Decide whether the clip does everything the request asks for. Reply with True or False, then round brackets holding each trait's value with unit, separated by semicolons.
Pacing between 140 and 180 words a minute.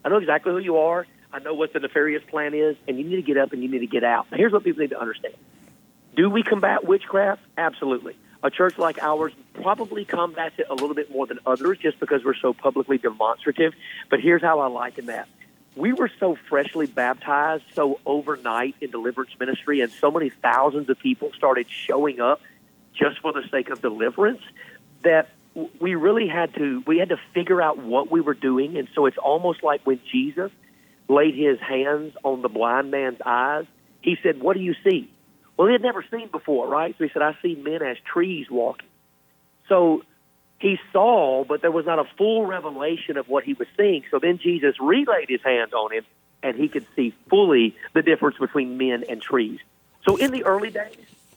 False (205 wpm)